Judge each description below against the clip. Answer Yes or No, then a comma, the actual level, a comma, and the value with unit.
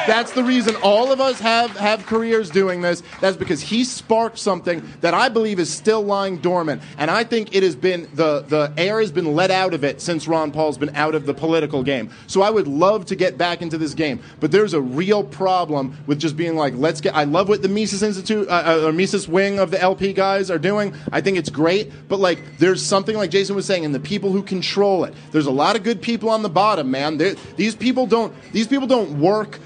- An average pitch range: Yes, average, 4.7 semitones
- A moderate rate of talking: No, fast, 245 wpm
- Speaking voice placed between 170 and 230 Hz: Yes, high, 190 Hz